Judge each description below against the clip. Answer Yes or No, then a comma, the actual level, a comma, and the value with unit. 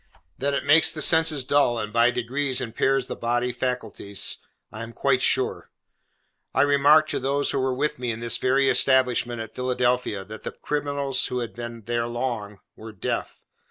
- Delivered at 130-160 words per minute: No, average, 180 wpm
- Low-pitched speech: Yes, low, 125 Hz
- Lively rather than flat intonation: No, average, 2.9 semitones